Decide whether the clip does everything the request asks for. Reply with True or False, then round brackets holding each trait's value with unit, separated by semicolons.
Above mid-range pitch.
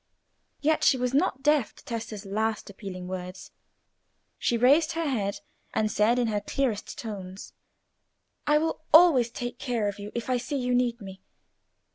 True (235 Hz)